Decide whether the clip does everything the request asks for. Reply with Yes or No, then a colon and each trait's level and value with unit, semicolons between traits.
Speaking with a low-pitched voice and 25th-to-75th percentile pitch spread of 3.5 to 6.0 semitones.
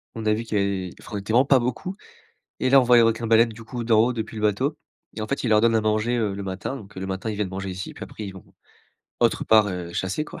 No: low, 110 Hz; average, 3.1 semitones